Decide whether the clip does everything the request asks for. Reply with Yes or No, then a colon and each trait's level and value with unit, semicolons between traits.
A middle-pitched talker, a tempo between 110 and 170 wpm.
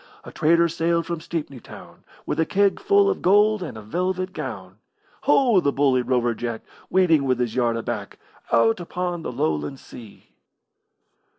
Yes: medium, 155 Hz; average, 165 wpm